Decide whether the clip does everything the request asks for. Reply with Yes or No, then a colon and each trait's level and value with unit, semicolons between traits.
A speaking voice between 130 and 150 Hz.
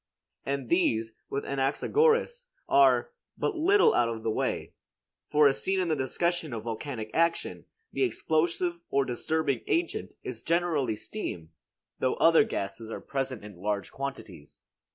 Yes: medium, 140 Hz